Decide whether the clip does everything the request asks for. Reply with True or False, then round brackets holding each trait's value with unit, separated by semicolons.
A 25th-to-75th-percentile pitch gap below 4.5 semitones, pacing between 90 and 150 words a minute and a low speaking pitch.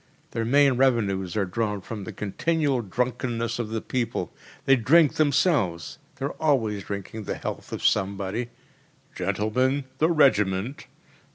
False (5.1 semitones; 140 wpm; 115 Hz)